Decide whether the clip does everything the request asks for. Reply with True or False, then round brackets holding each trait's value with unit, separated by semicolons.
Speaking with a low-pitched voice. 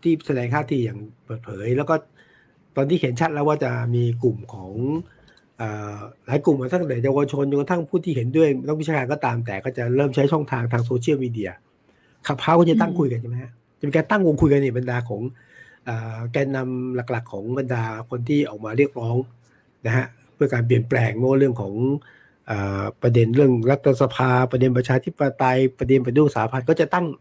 True (130 Hz)